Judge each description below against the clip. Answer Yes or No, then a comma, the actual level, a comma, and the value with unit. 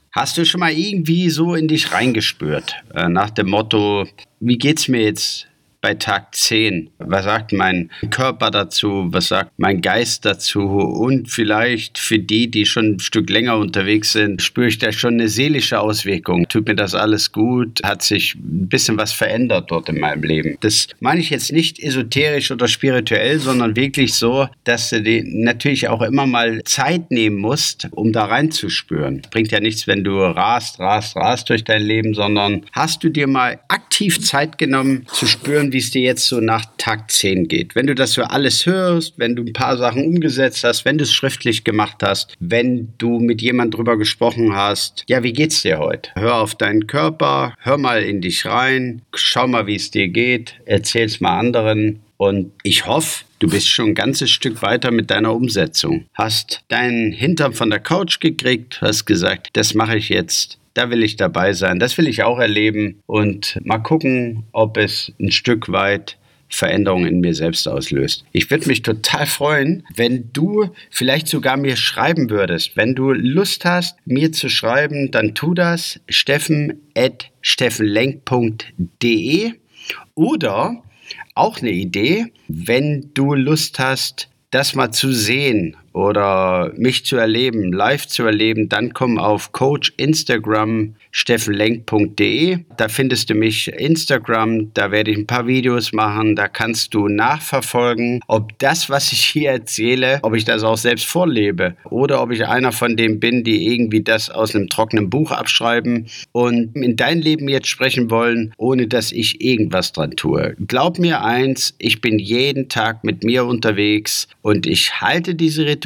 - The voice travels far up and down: No, average, 3.8 semitones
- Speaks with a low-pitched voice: Yes, low, 120 Hz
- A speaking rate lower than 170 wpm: No, average, 175 wpm